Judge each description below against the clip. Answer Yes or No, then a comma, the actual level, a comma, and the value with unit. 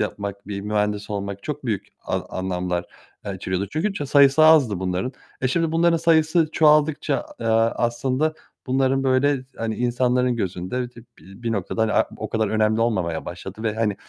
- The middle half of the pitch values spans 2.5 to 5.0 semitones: No, wide, 5.6 semitones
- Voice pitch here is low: Yes, low, 115 Hz